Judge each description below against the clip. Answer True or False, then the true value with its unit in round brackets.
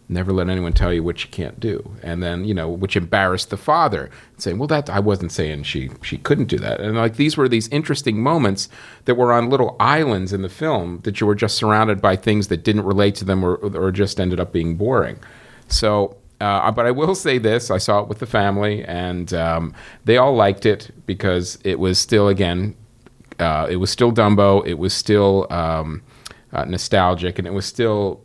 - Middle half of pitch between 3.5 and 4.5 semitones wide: True (3.8 semitones)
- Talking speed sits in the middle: False (215 wpm)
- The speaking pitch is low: True (100 Hz)